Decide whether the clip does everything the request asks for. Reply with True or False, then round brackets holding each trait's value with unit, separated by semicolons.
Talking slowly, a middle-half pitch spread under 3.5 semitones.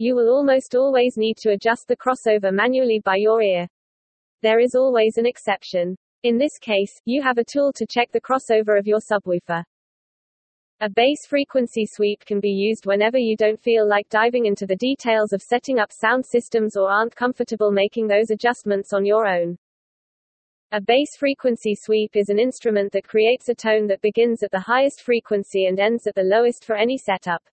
False (190 wpm; 3.0 semitones)